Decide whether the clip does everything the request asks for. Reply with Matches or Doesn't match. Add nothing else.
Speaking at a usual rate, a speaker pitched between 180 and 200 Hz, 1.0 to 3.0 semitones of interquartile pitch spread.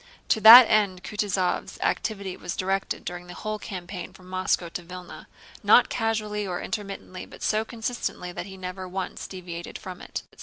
Matches